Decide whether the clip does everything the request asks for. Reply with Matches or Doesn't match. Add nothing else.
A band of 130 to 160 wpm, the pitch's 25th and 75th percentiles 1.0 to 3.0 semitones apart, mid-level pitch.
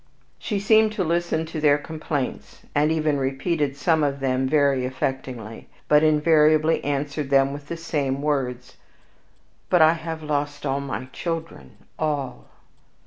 Matches